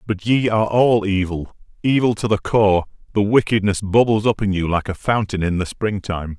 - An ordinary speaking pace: Yes, average, 190 wpm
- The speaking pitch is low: Yes, low, 105 Hz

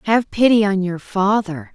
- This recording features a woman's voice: Yes, female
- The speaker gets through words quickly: No, average, 170 wpm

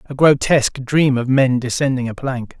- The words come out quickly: No, average, 185 wpm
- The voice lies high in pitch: No, low, 130 Hz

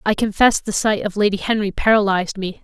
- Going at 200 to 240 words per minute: Yes, fast, 205 wpm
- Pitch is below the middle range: No, high, 205 Hz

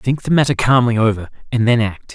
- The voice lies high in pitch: No, low, 120 Hz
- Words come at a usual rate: No, fast, 225 wpm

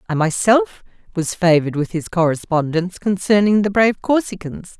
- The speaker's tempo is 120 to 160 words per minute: Yes, average, 140 wpm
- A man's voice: No, female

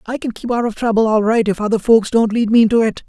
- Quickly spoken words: Yes, fast, 310 wpm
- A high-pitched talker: Yes, high, 225 Hz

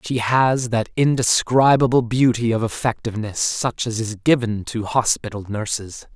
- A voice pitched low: Yes, low, 115 Hz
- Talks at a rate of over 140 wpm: No, slow, 135 wpm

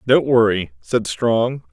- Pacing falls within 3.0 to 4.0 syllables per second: Yes, 3.4 syllables/s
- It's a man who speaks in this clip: Yes, male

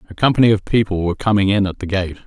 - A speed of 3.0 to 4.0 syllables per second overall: No, 7.6 syllables/s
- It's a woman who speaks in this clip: No, male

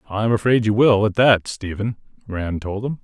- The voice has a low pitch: Yes, low, 110 Hz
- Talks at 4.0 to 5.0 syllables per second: Yes, 4.8 syllables/s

